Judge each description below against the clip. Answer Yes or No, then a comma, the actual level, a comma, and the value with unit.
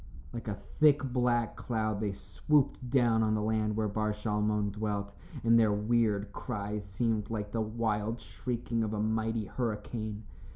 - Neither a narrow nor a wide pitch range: No, narrow, 1.9 semitones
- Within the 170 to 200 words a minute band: No, average, 160 wpm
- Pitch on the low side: Yes, low, 110 Hz